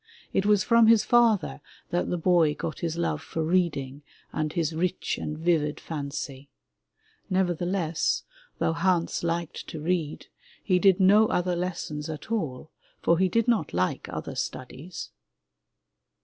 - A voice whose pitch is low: No, medium, 170 Hz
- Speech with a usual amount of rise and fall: Yes, average, 3.4 semitones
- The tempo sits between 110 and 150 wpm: Yes, average, 145 wpm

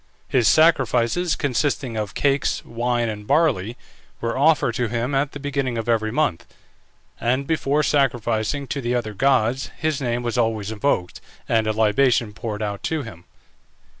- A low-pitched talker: Yes, low, 120 Hz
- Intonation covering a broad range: No, average, 3.9 semitones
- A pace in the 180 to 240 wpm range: No, average, 160 wpm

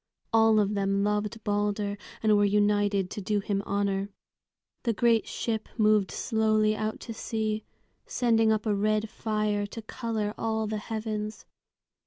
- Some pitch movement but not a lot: No, narrow, 1.2 semitones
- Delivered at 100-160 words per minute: Yes, average, 150 wpm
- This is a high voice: Yes, high, 215 Hz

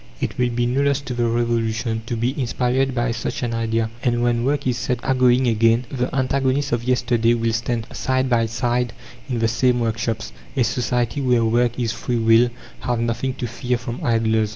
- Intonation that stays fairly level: Yes, narrow, 1.6 semitones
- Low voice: Yes, low, 120 Hz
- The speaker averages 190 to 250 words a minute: Yes, average, 200 wpm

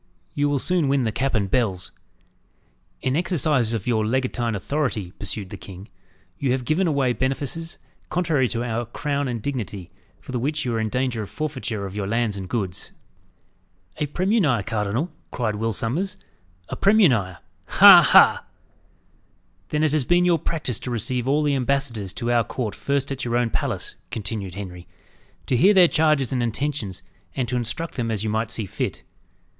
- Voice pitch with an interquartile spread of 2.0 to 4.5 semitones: No, average, 4.9 semitones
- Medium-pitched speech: No, low, 125 Hz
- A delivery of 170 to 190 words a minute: Yes, average, 180 wpm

